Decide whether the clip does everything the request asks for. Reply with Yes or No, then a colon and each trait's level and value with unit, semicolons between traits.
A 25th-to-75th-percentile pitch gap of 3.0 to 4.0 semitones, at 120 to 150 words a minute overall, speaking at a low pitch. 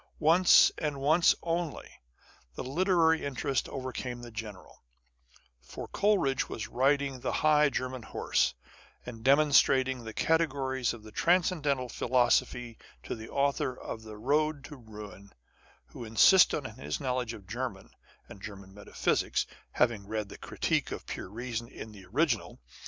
No: average, 4.7 semitones; average, 145 wpm; low, 130 Hz